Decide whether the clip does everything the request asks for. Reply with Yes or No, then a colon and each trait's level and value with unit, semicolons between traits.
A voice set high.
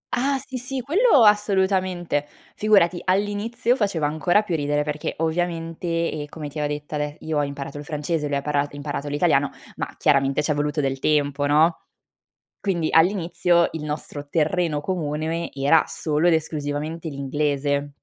No: medium, 155 Hz